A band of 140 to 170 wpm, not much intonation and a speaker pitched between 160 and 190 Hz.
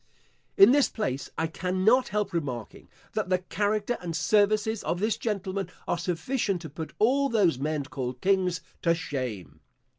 No: average, 155 wpm; average, 4.8 semitones; medium, 185 Hz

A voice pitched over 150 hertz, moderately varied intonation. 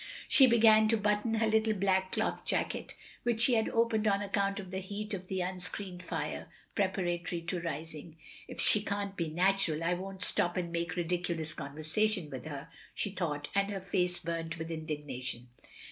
Yes: medium, 185 Hz; average, 3.6 semitones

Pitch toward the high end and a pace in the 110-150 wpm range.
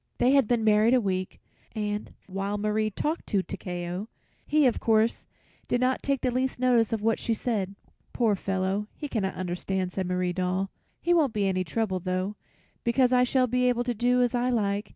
No: high, 215 Hz; average, 195 wpm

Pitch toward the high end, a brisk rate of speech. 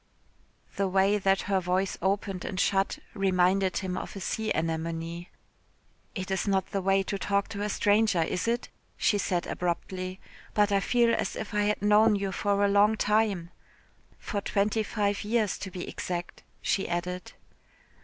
No: high, 195 Hz; average, 170 wpm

